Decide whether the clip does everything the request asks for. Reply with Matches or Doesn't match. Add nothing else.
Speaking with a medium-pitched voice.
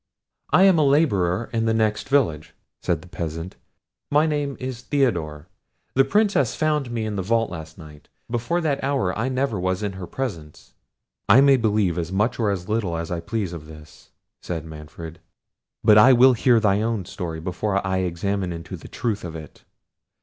Doesn't match